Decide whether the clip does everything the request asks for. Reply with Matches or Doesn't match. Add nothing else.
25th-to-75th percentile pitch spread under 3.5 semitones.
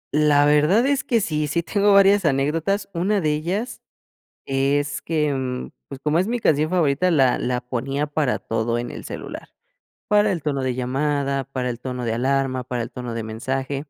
Doesn't match